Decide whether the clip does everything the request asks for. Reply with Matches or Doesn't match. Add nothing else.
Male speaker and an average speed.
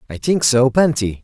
Matches